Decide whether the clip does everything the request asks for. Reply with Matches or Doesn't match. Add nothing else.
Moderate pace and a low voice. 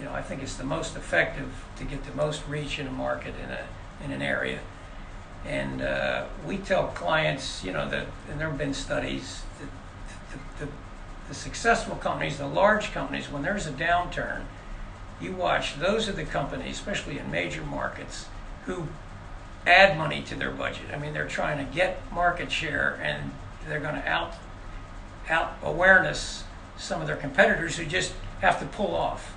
Matches